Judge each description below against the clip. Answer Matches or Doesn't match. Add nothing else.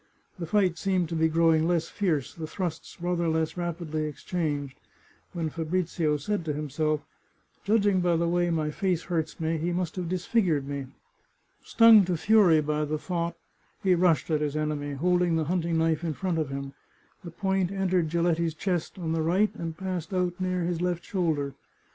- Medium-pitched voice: Matches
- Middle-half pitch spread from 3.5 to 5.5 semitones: Doesn't match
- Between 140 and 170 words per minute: Doesn't match